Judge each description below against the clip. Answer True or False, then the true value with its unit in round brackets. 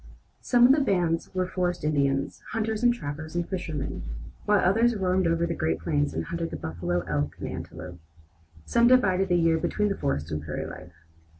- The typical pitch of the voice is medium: True (170 Hz)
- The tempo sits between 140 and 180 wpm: False (190 wpm)